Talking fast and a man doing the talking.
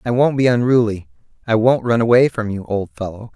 Yes: fast, 215 wpm; male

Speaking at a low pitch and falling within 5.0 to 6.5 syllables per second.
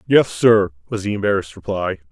Yes: low, 100 Hz; 6.1 syllables/s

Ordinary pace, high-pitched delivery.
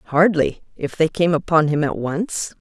No: average, 185 wpm; medium, 160 Hz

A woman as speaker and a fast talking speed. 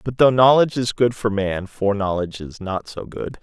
No: male; fast, 210 wpm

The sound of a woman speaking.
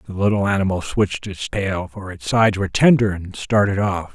No: male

